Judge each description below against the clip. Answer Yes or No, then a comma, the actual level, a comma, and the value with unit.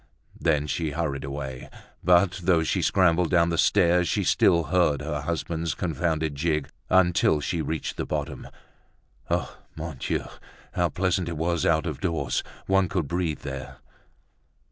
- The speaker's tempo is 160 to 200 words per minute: No, average, 150 wpm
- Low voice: Yes, very low, 80 Hz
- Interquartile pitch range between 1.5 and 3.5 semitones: Yes, average, 2.8 semitones